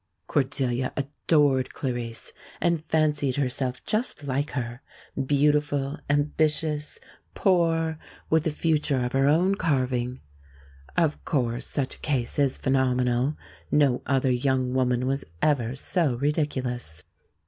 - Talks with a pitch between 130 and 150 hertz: Yes, medium, 140 Hz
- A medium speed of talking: No, slow, 115 wpm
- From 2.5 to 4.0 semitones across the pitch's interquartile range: Yes, average, 2.9 semitones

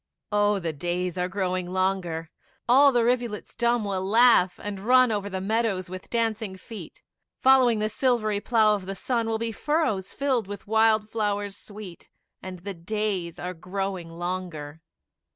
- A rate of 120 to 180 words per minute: Yes, average, 160 wpm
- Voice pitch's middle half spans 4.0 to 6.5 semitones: No, average, 3.5 semitones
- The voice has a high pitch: Yes, high, 205 Hz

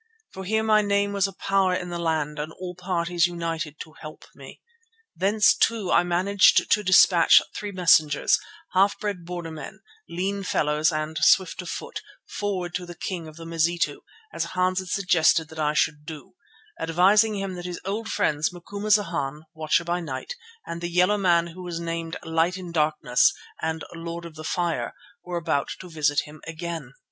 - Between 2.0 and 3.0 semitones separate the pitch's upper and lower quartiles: Yes, average, 2.7 semitones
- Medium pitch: Yes, medium, 175 Hz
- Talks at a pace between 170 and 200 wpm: Yes, average, 180 wpm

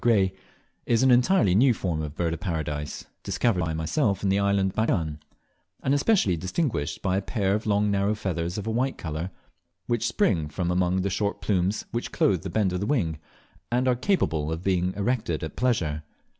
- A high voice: No, very low, 95 Hz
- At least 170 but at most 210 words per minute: Yes, average, 200 wpm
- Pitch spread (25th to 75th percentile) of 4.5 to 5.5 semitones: Yes, average, 5.2 semitones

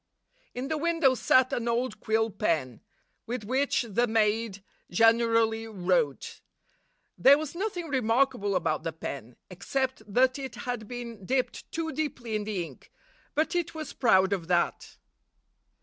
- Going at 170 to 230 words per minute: No, average, 145 wpm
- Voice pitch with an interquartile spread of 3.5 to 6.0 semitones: Yes, average, 4.8 semitones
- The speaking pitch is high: Yes, high, 230 Hz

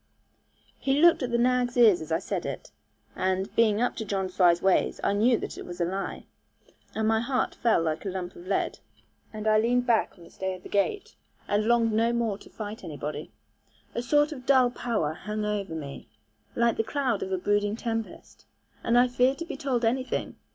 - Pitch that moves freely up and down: No, average, 4.3 semitones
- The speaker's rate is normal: No, fast, 210 wpm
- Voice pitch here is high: Yes, high, 220 Hz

